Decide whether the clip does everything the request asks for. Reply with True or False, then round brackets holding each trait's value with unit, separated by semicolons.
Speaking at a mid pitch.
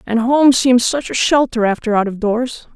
False (240 Hz)